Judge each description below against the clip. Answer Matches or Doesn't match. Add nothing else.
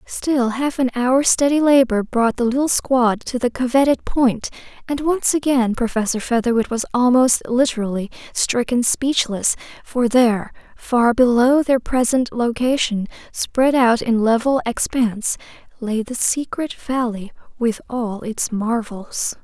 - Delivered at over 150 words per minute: Doesn't match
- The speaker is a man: Doesn't match